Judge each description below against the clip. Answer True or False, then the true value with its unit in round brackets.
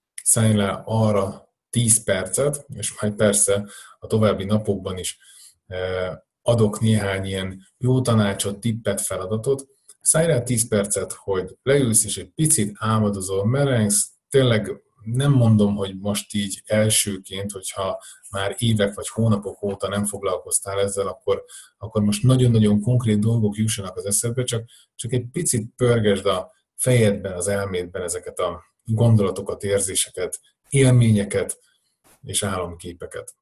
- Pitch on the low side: True (110 Hz)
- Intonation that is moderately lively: True (3.6 semitones)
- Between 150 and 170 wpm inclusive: False (130 wpm)